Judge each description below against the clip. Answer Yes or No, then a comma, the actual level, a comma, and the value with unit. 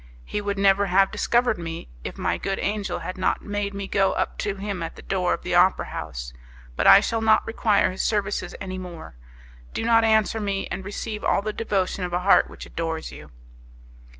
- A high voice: Yes, high, 200 Hz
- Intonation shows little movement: Yes, narrow, 2.3 semitones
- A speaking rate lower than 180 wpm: No, fast, 205 wpm